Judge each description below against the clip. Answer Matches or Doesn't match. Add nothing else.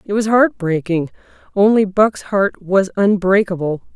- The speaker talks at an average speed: Doesn't match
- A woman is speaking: Matches